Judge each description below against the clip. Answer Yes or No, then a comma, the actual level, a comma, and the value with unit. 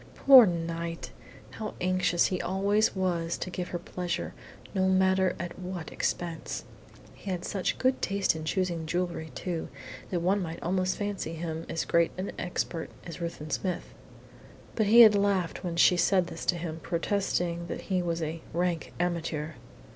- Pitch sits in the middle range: Yes, medium, 175 Hz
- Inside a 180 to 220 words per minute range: No, average, 165 wpm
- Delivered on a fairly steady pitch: Yes, narrow, 2.0 semitones